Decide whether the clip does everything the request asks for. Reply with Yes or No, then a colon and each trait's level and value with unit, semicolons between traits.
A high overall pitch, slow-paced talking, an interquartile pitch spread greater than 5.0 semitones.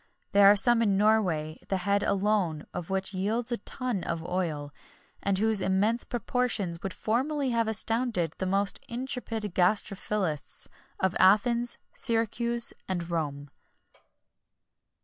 No: high, 200 Hz; slow, 130 wpm; average, 4.1 semitones